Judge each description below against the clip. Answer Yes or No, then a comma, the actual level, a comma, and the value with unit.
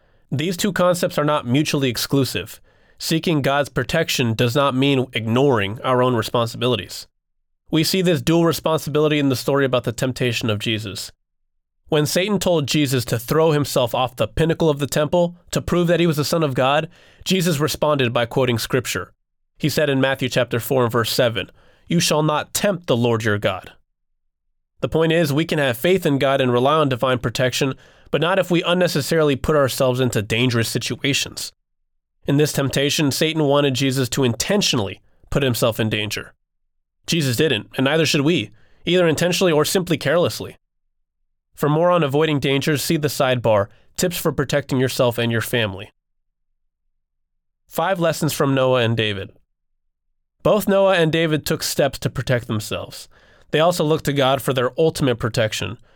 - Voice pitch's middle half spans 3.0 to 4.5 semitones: No, average, 5.2 semitones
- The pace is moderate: Yes, average, 170 wpm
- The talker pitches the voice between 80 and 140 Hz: Yes, low, 135 Hz